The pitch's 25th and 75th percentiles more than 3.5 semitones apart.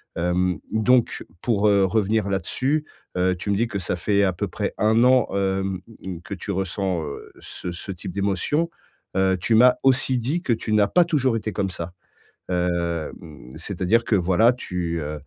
Yes: average, 4.2 semitones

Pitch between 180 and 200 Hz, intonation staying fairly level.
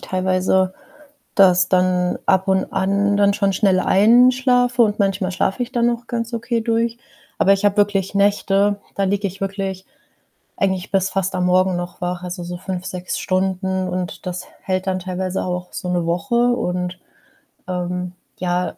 Yes: high, 190 Hz; narrow, 1.9 semitones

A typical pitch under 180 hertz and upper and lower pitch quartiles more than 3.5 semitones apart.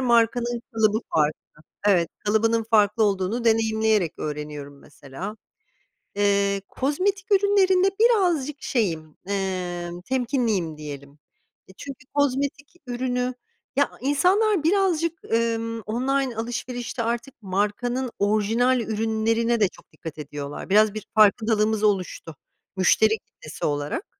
No: high, 225 Hz; average, 4.8 semitones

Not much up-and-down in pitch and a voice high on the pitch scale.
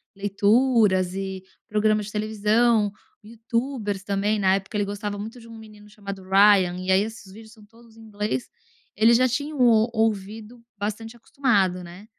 Yes: narrow, 2.2 semitones; high, 210 Hz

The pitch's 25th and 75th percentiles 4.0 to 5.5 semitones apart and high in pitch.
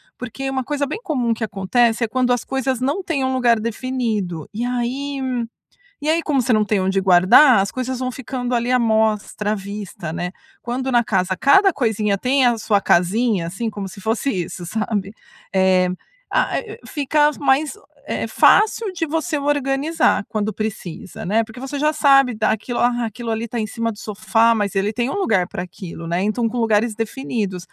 Yes: average, 4.3 semitones; high, 230 Hz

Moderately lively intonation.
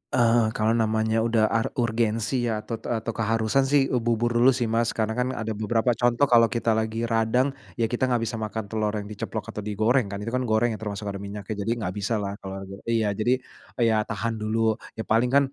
No: narrow, 1.6 semitones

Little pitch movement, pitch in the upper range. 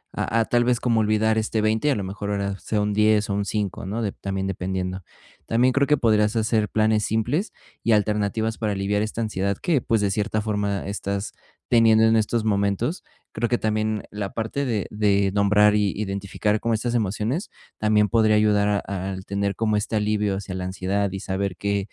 No: narrow, 1.8 semitones; low, 105 Hz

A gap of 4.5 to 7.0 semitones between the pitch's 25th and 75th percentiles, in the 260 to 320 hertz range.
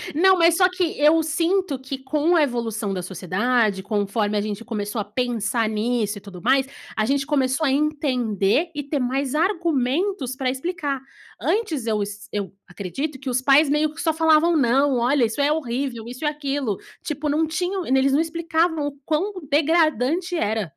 Yes: wide, 5.6 semitones; very high, 275 Hz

